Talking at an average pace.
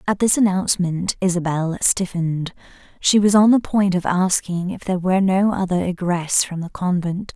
Yes: average, 170 wpm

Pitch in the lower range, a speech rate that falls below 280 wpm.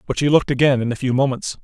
No: low, 130 Hz; fast, 295 wpm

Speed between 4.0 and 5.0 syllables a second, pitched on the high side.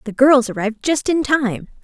No: 5.2 syllables/s; very high, 255 Hz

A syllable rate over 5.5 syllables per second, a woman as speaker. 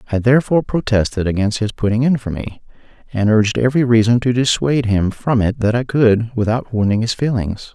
No: 5.9 syllables/s; male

